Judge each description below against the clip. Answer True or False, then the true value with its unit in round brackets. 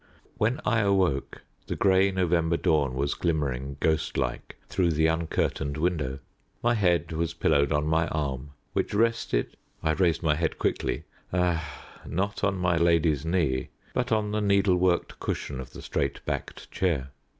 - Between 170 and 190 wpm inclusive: False (160 wpm)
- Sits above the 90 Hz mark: False (85 Hz)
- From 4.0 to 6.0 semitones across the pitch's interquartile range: True (4.3 semitones)